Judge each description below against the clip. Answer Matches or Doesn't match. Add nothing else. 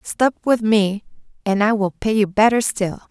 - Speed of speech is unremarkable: Matches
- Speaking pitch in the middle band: Doesn't match